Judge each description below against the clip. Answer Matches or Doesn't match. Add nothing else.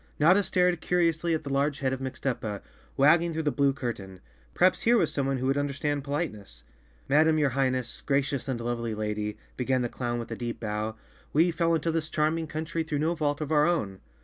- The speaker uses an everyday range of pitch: Matches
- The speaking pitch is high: Doesn't match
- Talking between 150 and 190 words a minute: Doesn't match